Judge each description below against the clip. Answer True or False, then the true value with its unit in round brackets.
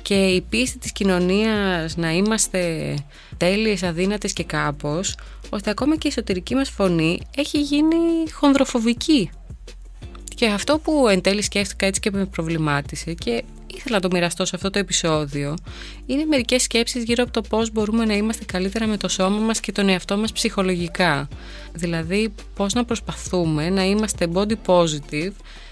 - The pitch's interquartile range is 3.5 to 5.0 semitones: True (4.6 semitones)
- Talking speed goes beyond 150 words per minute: True (160 wpm)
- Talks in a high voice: True (195 Hz)